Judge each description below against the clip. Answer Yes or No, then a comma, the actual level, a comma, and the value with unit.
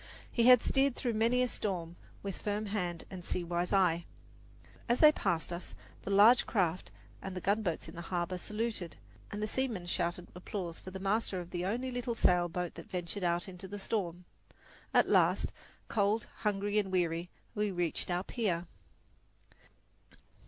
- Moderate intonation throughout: Yes, average, 3.5 semitones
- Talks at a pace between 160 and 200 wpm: Yes, average, 170 wpm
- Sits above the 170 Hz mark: Yes, high, 190 Hz